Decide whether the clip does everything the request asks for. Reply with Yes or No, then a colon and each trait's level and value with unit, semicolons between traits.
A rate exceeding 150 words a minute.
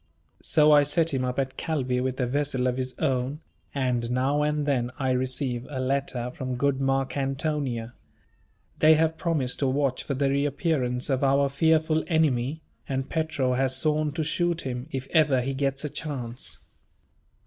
Yes: average, 170 wpm